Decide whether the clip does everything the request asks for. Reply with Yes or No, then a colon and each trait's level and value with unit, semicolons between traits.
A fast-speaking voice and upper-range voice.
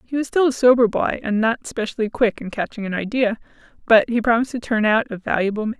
Yes: fast, 240 wpm; high, 230 Hz